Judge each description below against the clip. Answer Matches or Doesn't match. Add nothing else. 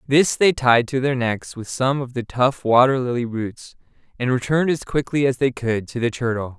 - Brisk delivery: Matches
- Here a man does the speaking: Matches